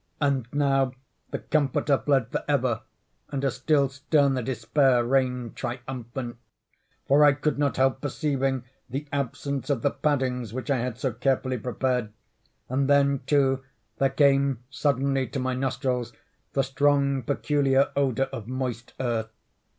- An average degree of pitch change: No, narrow, 1.9 semitones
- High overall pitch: No, low, 135 Hz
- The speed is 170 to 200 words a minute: No, average, 140 wpm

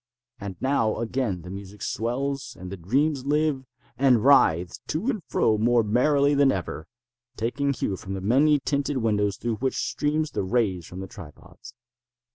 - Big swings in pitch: Yes, wide, 6.1 semitones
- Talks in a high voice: No, low, 120 Hz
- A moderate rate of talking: Yes, average, 165 wpm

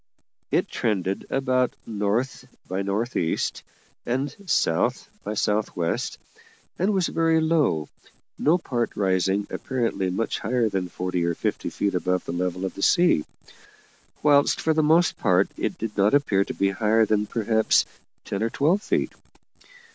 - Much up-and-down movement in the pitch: Yes, wide, 6.1 semitones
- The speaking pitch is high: No, low, 110 Hz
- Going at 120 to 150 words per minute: Yes, average, 145 wpm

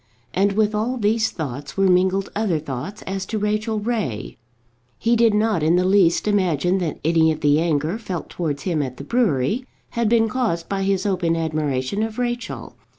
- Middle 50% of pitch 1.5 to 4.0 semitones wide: No, average, 5.3 semitones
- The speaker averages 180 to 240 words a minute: Yes, average, 185 wpm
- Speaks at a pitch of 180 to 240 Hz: Yes, high, 190 Hz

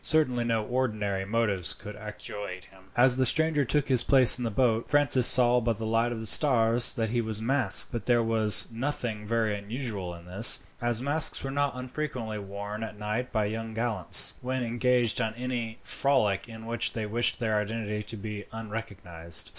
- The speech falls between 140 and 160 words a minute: No, average, 185 wpm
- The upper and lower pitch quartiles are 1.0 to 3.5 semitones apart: Yes, average, 2.8 semitones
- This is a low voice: Yes, low, 115 Hz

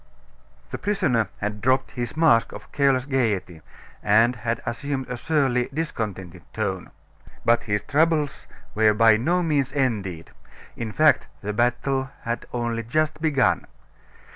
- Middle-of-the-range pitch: No, low, 120 Hz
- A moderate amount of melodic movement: Yes, average, 4.5 semitones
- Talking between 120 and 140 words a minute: Yes, slow, 135 wpm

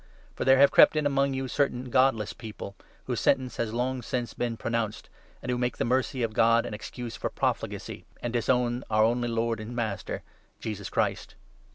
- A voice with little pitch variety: Yes, narrow, 2.2 semitones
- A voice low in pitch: Yes, low, 120 Hz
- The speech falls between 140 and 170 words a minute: No, average, 195 wpm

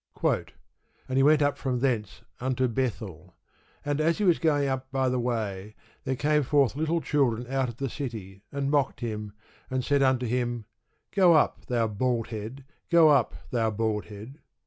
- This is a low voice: Yes, low, 130 Hz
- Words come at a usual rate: Yes, average, 175 wpm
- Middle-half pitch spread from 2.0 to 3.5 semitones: No, average, 3.9 semitones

